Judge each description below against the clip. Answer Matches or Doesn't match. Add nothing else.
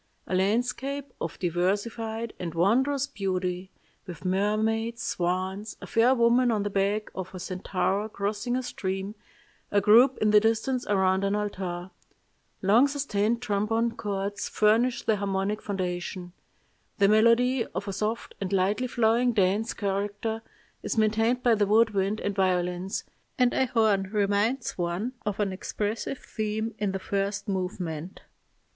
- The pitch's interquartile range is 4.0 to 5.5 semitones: Doesn't match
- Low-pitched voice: Doesn't match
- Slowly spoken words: Doesn't match